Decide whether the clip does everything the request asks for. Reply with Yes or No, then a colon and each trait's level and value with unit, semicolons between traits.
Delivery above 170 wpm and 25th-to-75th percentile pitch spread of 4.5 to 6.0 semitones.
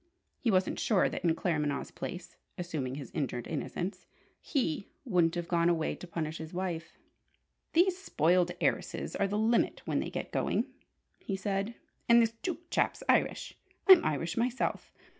No: average, 160 wpm; average, 5.1 semitones